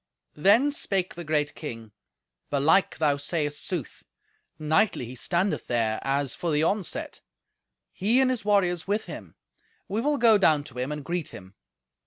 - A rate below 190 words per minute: Yes, average, 155 wpm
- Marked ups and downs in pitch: Yes, wide, 5.7 semitones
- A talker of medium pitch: Yes, medium, 160 Hz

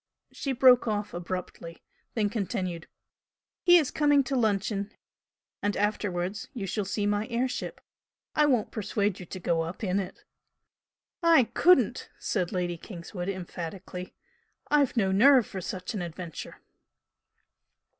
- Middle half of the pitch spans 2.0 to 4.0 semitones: No, average, 4.7 semitones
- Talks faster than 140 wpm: No, slow, 135 wpm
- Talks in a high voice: Yes, high, 205 Hz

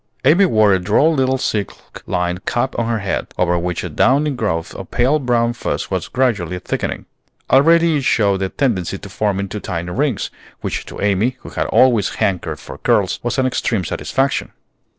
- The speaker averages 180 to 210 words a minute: Yes, average, 185 wpm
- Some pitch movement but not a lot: No, wide, 5.8 semitones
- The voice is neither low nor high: No, low, 110 Hz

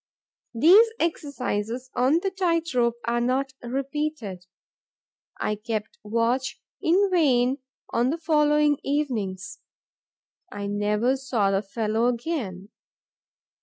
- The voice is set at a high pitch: Yes, very high, 250 Hz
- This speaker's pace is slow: Yes, slow, 105 wpm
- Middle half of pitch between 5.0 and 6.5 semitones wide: Yes, wide, 5.5 semitones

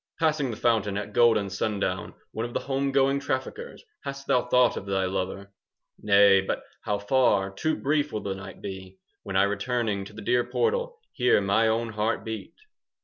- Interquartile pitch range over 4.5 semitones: Yes, average, 5.0 semitones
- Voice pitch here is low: Yes, low, 110 Hz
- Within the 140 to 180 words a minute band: No, average, 195 wpm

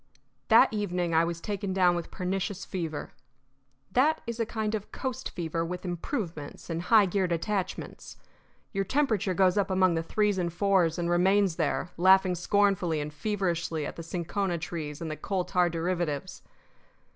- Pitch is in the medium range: Yes, medium, 180 Hz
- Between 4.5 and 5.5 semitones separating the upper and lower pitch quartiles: No, average, 3.0 semitones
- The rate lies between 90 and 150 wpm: No, average, 165 wpm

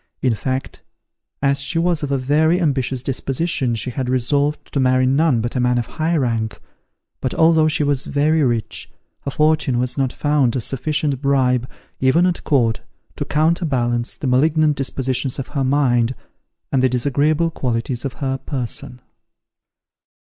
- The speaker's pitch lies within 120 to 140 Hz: Yes, low, 135 Hz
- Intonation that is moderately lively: Yes, average, 3.1 semitones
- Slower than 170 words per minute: Yes, average, 160 wpm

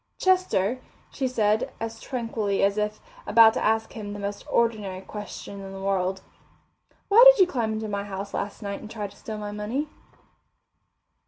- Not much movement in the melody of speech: Yes, narrow, 2.3 semitones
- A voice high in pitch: Yes, high, 210 Hz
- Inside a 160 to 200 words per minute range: Yes, average, 175 wpm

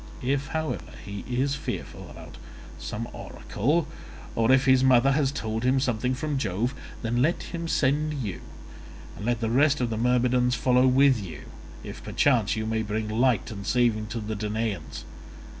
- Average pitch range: Yes, average, 3.4 semitones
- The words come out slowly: No, average, 170 wpm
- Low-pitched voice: Yes, low, 125 Hz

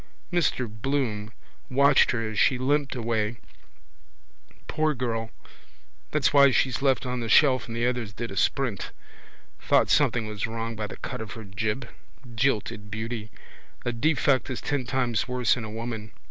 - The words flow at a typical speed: Yes, average, 160 wpm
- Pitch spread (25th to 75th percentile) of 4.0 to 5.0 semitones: No, average, 3.2 semitones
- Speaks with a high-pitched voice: No, low, 120 Hz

